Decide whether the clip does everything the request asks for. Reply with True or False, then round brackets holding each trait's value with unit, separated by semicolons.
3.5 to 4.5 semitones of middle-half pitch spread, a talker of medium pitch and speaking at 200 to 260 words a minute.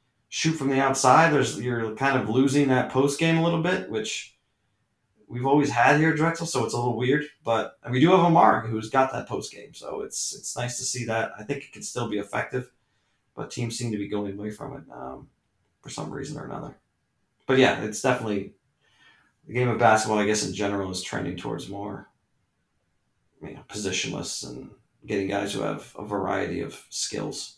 False (4.2 semitones; 125 Hz; 205 wpm)